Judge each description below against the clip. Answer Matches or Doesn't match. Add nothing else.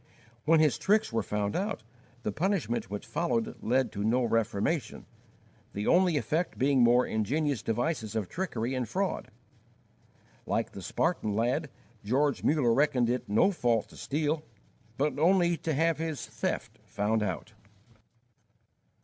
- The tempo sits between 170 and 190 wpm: Doesn't match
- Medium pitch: Doesn't match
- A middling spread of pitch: Doesn't match